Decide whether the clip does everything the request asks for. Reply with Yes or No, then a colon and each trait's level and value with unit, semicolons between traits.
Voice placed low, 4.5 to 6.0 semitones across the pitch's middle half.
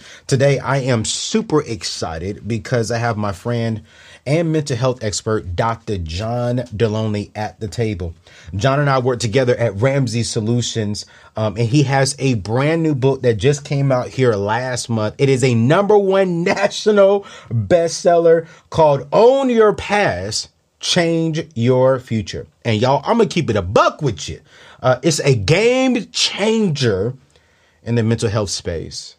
Yes: low, 130 Hz; wide, 5.6 semitones